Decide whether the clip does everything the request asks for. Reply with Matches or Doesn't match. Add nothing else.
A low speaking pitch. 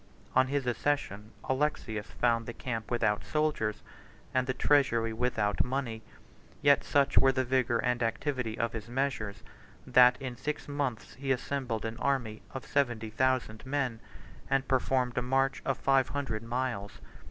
Matches